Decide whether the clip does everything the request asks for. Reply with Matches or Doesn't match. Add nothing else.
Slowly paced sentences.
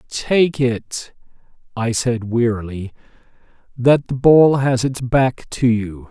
Matches